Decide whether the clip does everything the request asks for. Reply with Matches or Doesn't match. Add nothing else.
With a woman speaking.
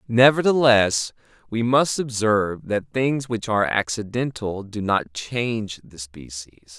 Doesn't match